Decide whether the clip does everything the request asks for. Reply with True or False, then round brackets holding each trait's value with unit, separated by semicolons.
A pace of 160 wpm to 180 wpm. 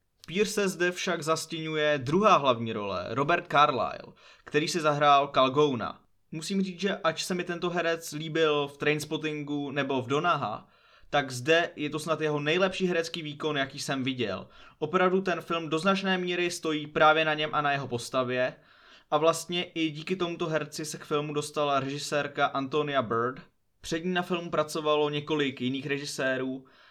True (165 wpm)